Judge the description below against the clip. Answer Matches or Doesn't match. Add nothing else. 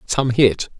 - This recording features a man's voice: Matches